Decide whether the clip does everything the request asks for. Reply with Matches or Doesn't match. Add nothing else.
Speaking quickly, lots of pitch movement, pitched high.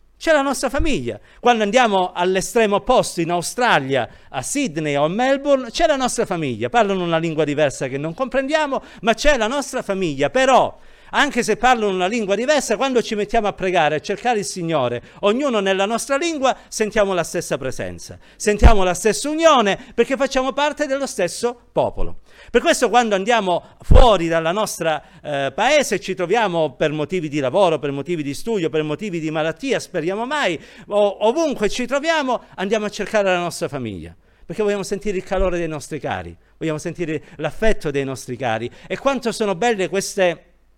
Matches